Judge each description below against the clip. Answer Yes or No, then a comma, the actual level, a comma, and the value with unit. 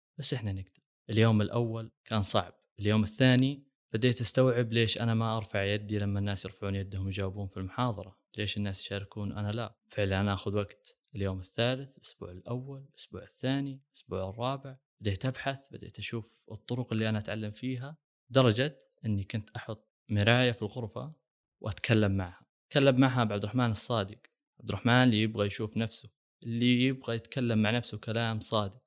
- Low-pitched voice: Yes, low, 115 Hz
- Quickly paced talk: Yes, fast, 160 wpm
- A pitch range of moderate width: Yes, average, 3.6 semitones